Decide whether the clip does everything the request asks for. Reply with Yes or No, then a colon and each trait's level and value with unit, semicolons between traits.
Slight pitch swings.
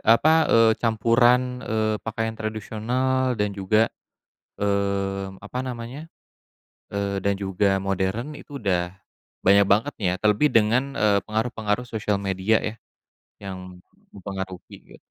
No: average, 3.0 semitones